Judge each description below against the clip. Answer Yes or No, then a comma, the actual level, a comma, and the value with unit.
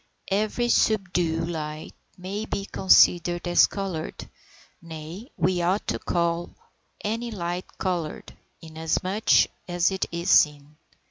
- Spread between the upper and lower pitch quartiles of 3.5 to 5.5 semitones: No, average, 3.0 semitones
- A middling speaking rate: No, slow, 115 wpm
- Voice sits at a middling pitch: Yes, medium, 175 Hz